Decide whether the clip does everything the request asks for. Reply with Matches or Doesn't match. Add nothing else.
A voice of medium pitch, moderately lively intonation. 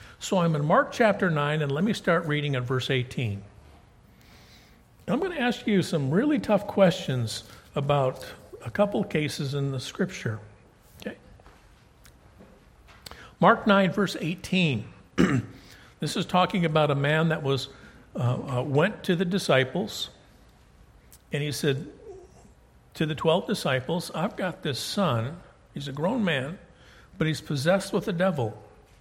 Doesn't match